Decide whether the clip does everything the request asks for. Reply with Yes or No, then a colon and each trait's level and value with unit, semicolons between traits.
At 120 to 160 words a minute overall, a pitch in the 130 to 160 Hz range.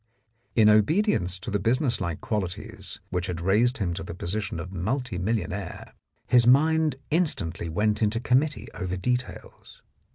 No: average, 150 wpm; low, 105 Hz